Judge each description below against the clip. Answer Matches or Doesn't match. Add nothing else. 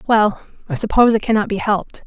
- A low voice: Doesn't match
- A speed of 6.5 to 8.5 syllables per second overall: Matches